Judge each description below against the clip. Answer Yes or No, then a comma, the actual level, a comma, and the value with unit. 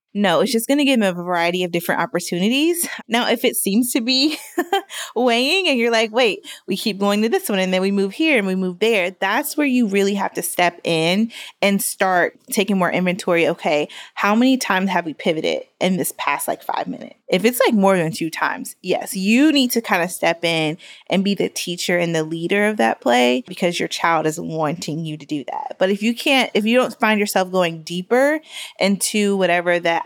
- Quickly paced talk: Yes, fast, 225 wpm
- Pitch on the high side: Yes, high, 200 Hz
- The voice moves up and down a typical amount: No, wide, 5.8 semitones